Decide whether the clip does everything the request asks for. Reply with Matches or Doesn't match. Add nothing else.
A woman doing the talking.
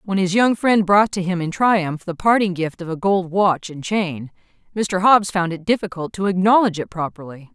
Matches